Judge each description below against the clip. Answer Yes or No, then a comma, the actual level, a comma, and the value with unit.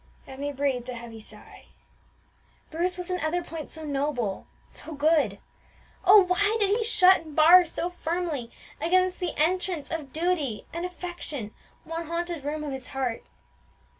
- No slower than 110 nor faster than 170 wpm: Yes, average, 155 wpm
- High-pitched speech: Yes, very high, 325 Hz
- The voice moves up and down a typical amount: Yes, average, 4.3 semitones